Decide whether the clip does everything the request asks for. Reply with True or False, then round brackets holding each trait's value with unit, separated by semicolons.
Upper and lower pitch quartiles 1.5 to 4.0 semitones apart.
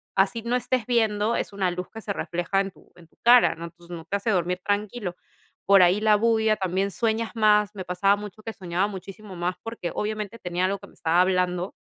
True (3.0 semitones)